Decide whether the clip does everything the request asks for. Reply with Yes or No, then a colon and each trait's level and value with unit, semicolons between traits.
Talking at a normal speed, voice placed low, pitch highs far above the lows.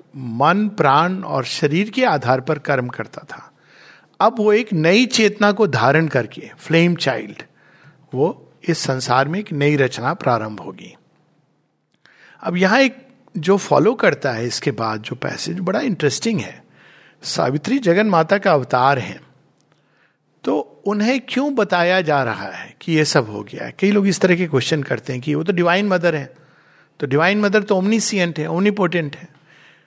No: average, 170 wpm; medium, 170 Hz; wide, 6.2 semitones